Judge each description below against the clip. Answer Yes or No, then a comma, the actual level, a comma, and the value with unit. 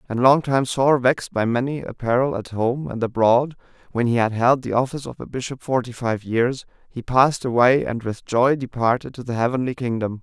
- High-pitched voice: No, low, 125 Hz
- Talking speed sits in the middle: No, fast, 210 wpm